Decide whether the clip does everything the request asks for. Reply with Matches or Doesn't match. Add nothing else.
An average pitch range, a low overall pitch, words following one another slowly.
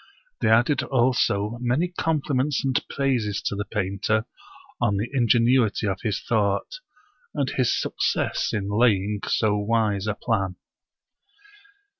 Matches